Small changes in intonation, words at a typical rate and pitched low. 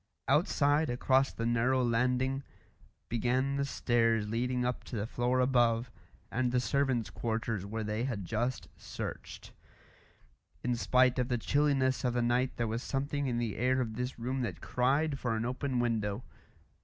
Yes: narrow, 2.2 semitones; average, 165 wpm; low, 125 Hz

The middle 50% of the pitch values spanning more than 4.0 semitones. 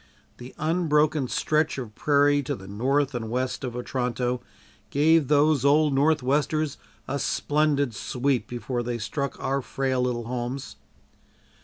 No: average, 3.2 semitones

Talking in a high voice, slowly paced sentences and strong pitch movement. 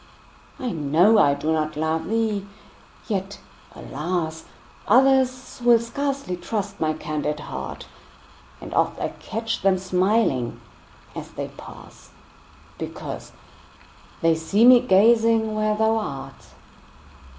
Yes: high, 200 Hz; slow, 115 wpm; wide, 6.0 semitones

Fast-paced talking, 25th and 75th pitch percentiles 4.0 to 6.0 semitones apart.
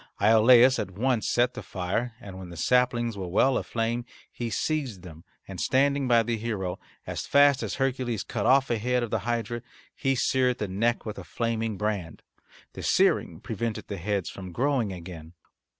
No: average, 180 wpm; average, 4.3 semitones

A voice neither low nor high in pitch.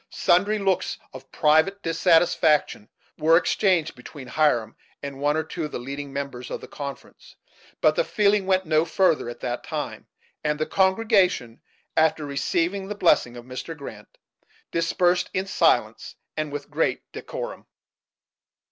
Yes: medium, 160 Hz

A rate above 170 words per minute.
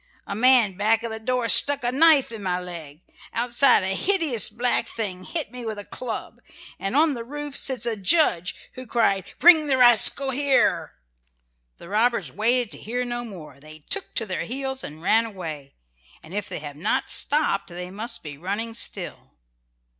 Yes: average, 185 wpm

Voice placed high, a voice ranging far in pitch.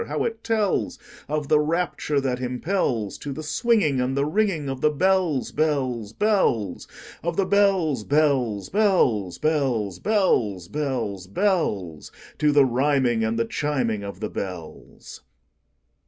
No: medium, 140 Hz; wide, 7.0 semitones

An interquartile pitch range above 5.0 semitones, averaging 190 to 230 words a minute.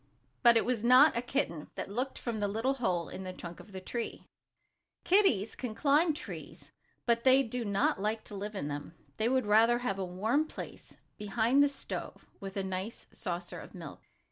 No: average, 4.6 semitones; average, 195 wpm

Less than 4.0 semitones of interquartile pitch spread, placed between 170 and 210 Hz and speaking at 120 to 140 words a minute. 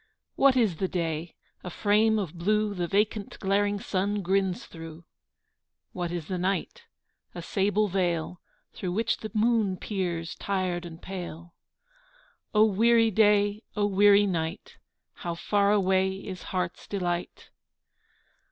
Yes: average, 2.8 semitones; high, 190 Hz; slow, 135 wpm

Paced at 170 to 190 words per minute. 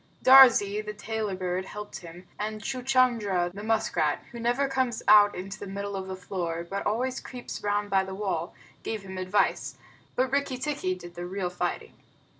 Yes: average, 180 wpm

